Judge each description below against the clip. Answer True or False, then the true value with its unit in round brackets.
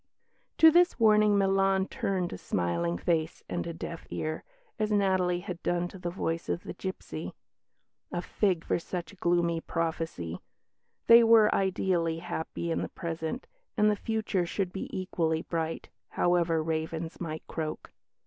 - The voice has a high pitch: False (175 Hz)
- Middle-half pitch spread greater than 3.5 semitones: False (3.0 semitones)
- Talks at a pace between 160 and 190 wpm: False (150 wpm)